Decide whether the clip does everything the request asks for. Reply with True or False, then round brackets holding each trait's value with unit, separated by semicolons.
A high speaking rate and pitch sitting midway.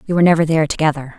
True (255 wpm; 160 Hz)